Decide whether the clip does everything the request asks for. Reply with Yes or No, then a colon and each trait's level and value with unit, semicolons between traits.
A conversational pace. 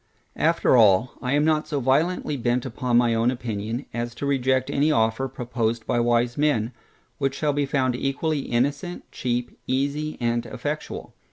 Yes: average, 165 wpm